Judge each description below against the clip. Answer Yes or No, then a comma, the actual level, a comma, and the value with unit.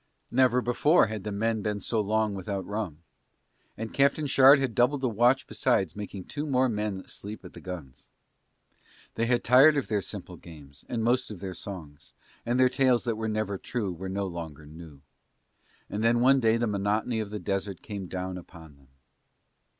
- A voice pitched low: Yes, low, 105 Hz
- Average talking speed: Yes, average, 190 wpm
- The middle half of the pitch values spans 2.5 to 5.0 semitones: Yes, average, 4.5 semitones